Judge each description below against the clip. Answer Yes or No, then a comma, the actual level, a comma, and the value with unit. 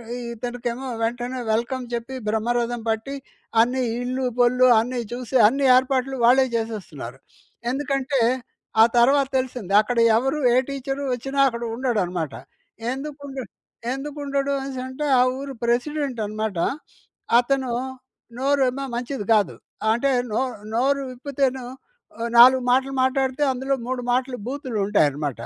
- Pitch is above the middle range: Yes, very high, 255 Hz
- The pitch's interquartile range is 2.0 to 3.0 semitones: Yes, narrow, 2.4 semitones